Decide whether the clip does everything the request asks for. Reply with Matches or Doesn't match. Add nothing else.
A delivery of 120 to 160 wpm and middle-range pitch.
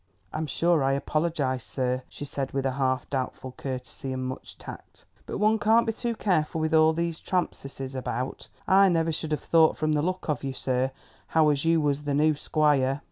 Doesn't match